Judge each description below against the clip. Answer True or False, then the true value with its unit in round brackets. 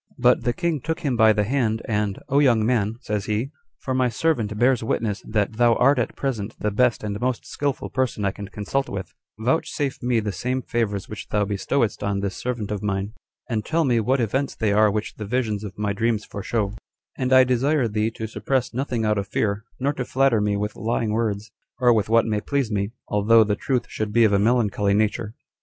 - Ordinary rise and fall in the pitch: True (3.4 semitones)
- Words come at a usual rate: False (220 wpm)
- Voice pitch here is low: True (110 Hz)